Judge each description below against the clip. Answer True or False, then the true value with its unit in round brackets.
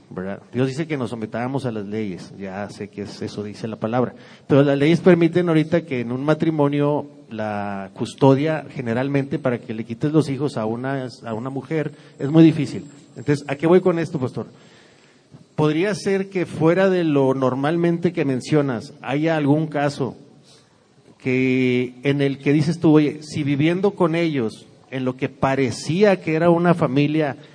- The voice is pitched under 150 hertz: True (140 Hz)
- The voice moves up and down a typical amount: True (3.9 semitones)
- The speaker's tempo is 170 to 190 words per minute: True (175 wpm)